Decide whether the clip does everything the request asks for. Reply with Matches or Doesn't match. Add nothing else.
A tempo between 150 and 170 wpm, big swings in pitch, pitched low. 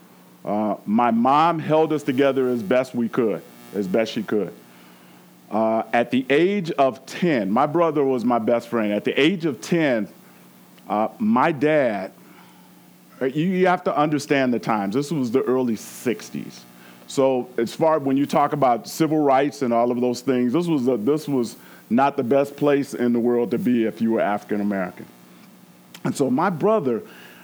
Doesn't match